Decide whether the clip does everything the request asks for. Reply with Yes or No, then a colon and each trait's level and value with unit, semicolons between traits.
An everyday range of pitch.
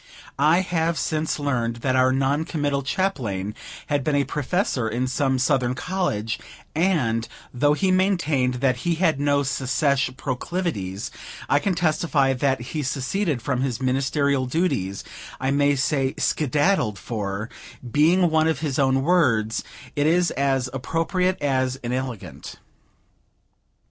Yes: average, 4.0 semitones